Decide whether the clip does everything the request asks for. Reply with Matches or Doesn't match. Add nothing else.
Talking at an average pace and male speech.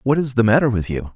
Doesn't match